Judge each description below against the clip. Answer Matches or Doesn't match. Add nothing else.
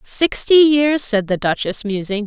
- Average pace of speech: Matches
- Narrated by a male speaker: Doesn't match